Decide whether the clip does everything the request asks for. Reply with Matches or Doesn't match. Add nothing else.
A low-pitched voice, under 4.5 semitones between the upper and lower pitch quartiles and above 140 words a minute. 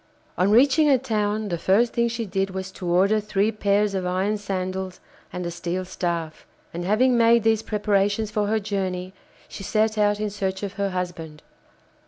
Doesn't match